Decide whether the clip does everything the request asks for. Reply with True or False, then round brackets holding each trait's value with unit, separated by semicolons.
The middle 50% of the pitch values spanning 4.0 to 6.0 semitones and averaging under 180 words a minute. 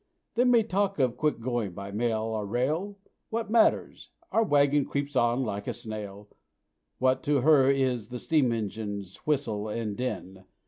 True (5.4 semitones; 170 wpm)